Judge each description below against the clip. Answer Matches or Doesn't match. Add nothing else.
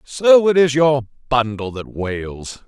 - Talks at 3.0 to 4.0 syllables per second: Matches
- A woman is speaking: Doesn't match